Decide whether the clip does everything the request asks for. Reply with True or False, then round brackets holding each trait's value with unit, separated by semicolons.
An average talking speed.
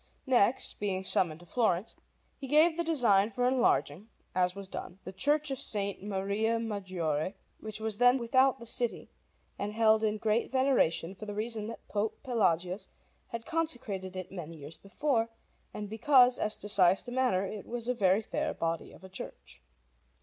True (175 wpm)